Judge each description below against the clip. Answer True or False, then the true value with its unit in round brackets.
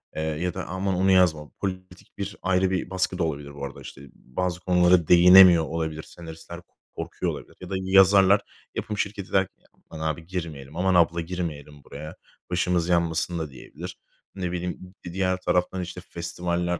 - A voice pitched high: False (90 Hz)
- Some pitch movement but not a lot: False (2.2 semitones)